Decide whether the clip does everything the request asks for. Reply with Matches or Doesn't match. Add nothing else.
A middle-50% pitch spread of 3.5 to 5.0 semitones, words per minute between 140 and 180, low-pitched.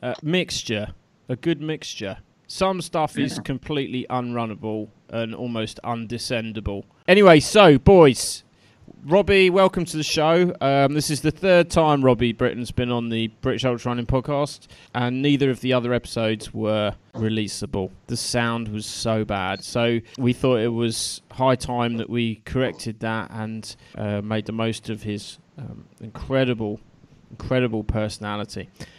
Matches